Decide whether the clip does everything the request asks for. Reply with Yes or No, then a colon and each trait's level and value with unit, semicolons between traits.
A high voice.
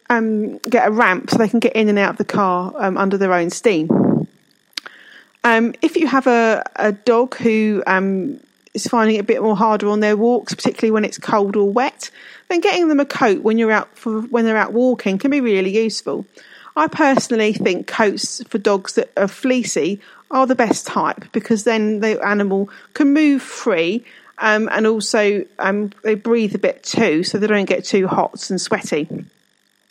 Yes: high, 220 Hz